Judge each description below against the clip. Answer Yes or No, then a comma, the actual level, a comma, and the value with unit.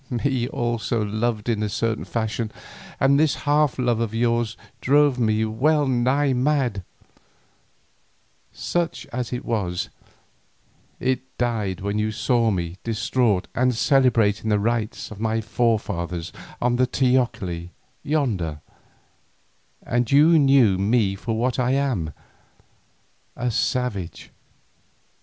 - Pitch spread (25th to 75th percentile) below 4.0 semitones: Yes, average, 3.3 semitones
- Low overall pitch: Yes, low, 120 Hz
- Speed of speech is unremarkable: No, slow, 120 wpm